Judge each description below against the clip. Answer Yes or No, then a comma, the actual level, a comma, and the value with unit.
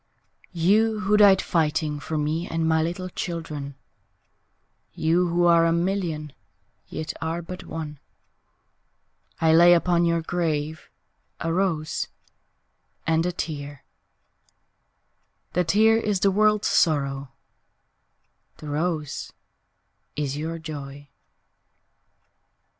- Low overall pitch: No, medium, 165 Hz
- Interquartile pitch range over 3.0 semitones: No, average, 2.7 semitones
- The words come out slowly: Yes, slow, 105 wpm